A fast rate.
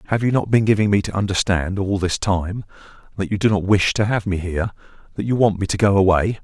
Yes: fast, 240 wpm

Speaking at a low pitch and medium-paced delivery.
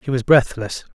Yes: low, 125 Hz; average, 190 wpm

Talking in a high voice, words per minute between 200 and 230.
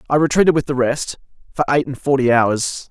No: low, 135 Hz; fast, 205 wpm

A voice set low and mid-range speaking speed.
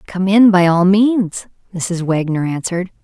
No: medium, 185 Hz; average, 160 wpm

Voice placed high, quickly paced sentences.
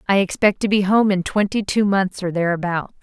Yes: high, 195 Hz; fast, 220 wpm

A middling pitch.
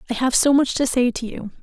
No: very high, 250 Hz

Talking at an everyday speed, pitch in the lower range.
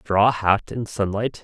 Yes: average, 170 wpm; low, 105 Hz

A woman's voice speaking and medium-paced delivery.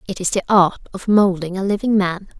No: female; fast, 225 wpm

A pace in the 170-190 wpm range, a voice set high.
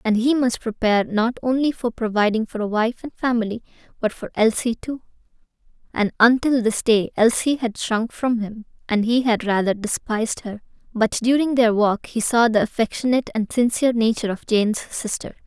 Yes: average, 180 wpm; high, 230 Hz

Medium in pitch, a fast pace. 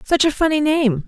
No: very high, 285 Hz; fast, 225 wpm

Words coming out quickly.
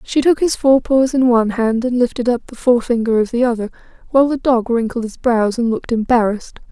Yes: fast, 225 wpm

